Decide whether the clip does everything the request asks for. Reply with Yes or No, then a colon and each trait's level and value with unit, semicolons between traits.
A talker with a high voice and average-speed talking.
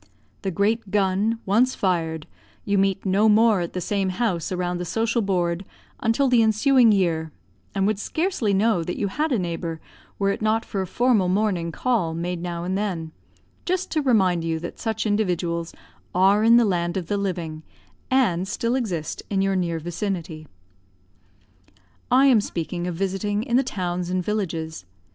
Yes: high, 195 Hz; average, 175 wpm